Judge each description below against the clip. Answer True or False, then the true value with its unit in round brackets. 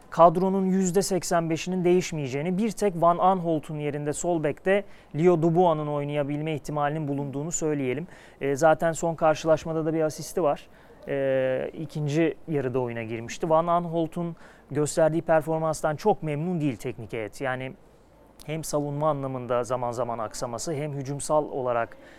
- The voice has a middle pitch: True (155 Hz)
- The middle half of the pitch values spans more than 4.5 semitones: False (3.1 semitones)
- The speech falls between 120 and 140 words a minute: True (135 wpm)